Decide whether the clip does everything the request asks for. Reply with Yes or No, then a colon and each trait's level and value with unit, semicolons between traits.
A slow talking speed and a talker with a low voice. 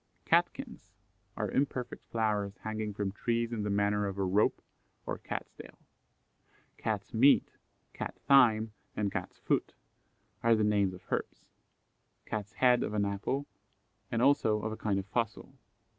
No: average, 150 wpm; low, 110 Hz